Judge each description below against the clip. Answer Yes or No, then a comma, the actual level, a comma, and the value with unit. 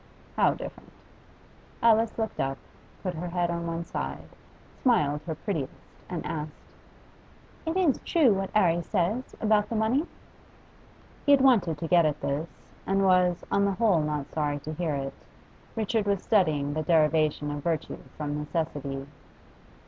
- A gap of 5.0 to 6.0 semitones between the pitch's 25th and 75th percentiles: Yes, wide, 5.6 semitones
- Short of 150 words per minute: No, average, 155 wpm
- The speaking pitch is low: No, medium, 170 Hz